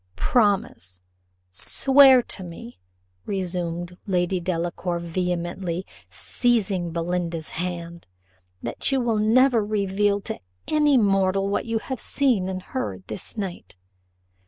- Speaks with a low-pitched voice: No, medium, 185 Hz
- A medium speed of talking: No, slow, 110 wpm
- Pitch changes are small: No, average, 3.9 semitones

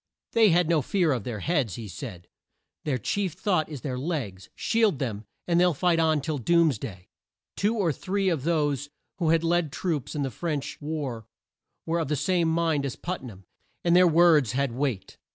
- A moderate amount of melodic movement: Yes, average, 4.9 semitones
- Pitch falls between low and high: Yes, medium, 155 Hz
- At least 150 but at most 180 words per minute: No, average, 195 wpm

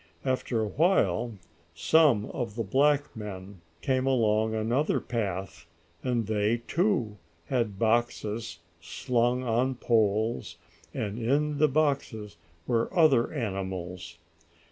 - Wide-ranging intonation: No, average, 4.0 semitones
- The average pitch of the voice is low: Yes, low, 115 Hz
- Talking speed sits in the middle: No, slow, 105 wpm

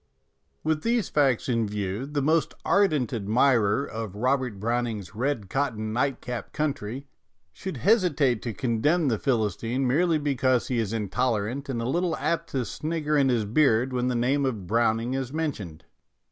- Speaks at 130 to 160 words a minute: No, average, 175 wpm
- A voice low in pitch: Yes, low, 125 Hz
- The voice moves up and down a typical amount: Yes, average, 4.3 semitones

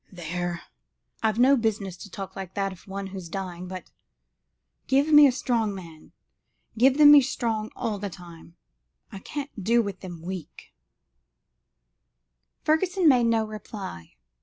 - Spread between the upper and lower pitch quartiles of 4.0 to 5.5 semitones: Yes, average, 4.9 semitones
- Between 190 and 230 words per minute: No, average, 145 wpm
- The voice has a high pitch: Yes, high, 205 Hz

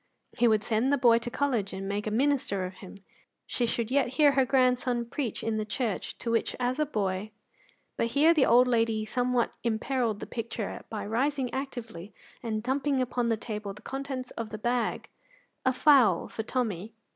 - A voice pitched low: No, high, 235 Hz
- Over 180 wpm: Yes, average, 190 wpm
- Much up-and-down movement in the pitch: No, average, 3.1 semitones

